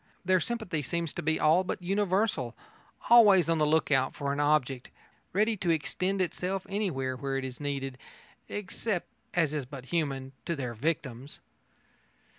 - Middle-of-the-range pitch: Yes, medium, 155 Hz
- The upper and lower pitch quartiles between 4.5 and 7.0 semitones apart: Yes, wide, 5.5 semitones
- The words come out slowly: No, average, 160 wpm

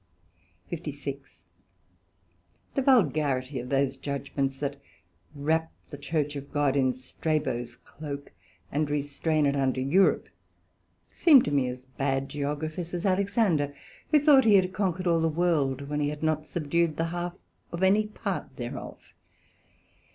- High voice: No, medium, 150 Hz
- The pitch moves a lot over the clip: No, average, 3.7 semitones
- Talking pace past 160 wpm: No, average, 140 wpm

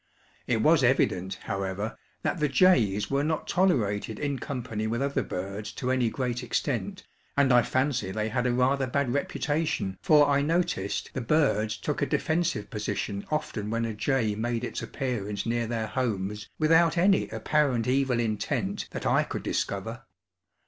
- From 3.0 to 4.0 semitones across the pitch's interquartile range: No, average, 4.9 semitones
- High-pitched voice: No, low, 125 Hz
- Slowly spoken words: No, average, 165 wpm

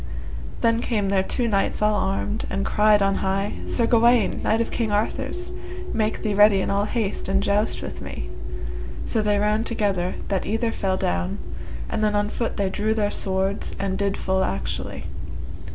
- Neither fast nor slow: Yes, average, 180 wpm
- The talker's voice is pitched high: Yes, high, 205 Hz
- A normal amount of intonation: No, narrow, 2.0 semitones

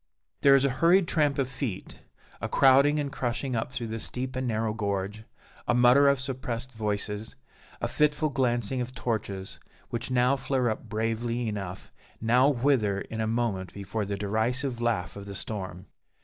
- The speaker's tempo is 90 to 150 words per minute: No, average, 170 wpm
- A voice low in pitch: Yes, low, 120 Hz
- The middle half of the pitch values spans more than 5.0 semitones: No, average, 3.5 semitones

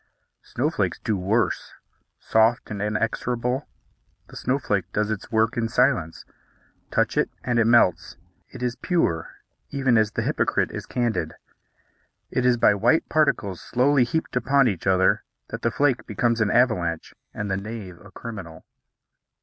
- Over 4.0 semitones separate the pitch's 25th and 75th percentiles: No, average, 3.7 semitones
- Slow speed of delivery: No, average, 150 wpm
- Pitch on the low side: Yes, low, 115 Hz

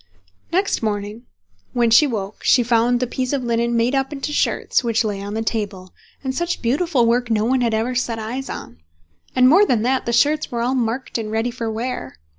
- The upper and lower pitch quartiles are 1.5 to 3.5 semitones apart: Yes, narrow, 2.6 semitones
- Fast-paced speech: Yes, fast, 210 wpm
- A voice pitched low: No, high, 235 Hz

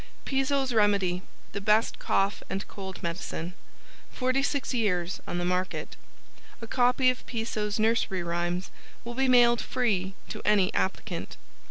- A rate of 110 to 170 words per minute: Yes, slow, 135 wpm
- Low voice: No, high, 210 Hz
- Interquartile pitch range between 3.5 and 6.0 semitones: Yes, average, 5.1 semitones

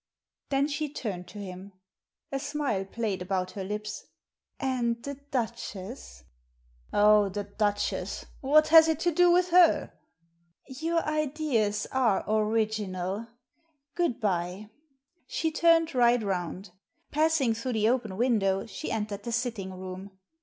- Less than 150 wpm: Yes, average, 140 wpm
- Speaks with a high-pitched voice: Yes, high, 220 Hz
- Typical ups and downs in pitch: No, wide, 6.1 semitones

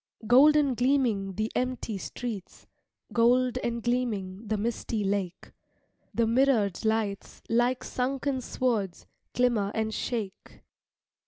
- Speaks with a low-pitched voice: No, high, 235 Hz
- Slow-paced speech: Yes, slow, 110 wpm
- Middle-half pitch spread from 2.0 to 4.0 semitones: Yes, average, 3.5 semitones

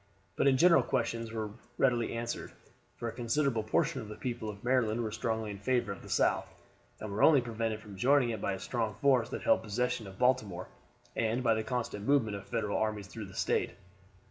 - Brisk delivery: Yes, fast, 210 wpm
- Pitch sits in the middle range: No, low, 115 Hz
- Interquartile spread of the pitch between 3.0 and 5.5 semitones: No, narrow, 2.6 semitones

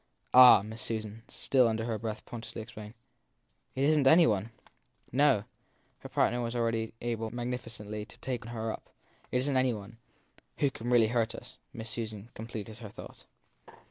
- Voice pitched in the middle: No, low, 115 Hz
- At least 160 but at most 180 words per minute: Yes, average, 175 wpm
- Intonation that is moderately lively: No, narrow, 2.0 semitones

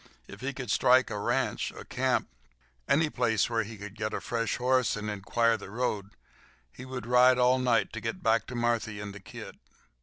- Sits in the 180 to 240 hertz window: No, low, 115 Hz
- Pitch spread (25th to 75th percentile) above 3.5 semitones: No, average, 3.2 semitones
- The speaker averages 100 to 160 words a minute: No, average, 190 wpm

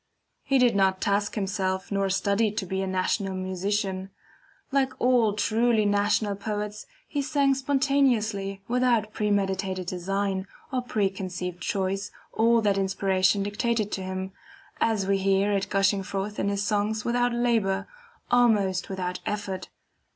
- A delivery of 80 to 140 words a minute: Yes, slow, 135 wpm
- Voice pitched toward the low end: No, high, 200 Hz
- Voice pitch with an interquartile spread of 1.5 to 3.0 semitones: Yes, narrow, 2.6 semitones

